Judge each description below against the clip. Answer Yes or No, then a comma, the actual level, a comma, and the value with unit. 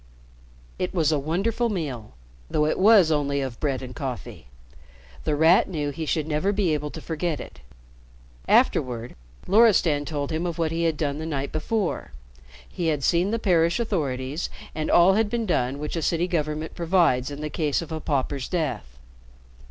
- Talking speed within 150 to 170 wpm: No, average, 180 wpm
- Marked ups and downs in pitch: No, average, 3.5 semitones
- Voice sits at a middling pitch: Yes, medium, 155 Hz